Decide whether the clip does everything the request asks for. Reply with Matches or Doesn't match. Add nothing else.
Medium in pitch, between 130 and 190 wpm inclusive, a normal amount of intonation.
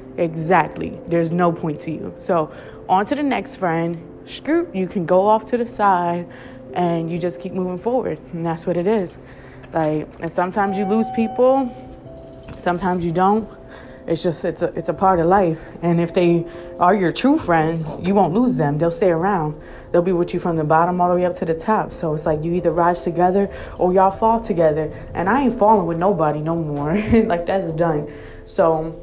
Doesn't match